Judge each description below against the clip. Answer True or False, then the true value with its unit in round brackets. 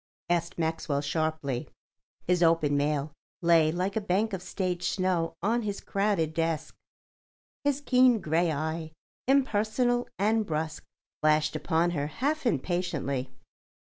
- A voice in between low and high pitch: True (170 Hz)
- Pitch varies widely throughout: False (4.7 semitones)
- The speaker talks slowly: True (125 wpm)